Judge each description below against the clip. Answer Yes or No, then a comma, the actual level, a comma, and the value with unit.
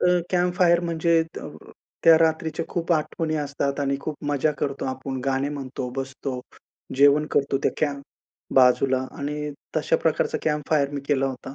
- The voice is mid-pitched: Yes, medium, 145 Hz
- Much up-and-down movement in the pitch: No, average, 2.8 semitones